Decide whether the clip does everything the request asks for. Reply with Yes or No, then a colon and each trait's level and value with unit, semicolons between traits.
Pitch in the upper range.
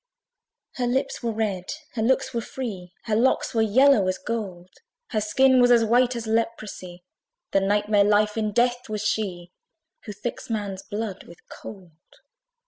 Yes: high, 215 Hz